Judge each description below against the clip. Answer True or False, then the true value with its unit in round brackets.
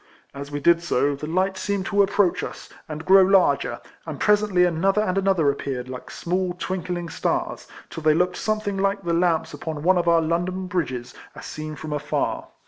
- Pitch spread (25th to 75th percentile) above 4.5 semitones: False (3.6 semitones)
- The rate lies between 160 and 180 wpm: False (190 wpm)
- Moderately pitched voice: True (175 Hz)